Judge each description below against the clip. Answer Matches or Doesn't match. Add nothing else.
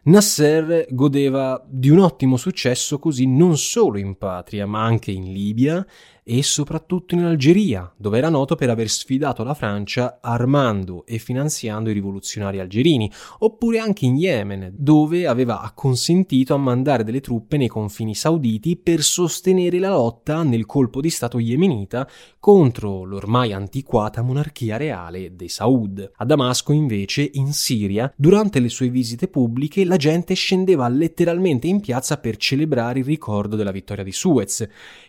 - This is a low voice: Matches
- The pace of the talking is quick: Doesn't match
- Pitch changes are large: Matches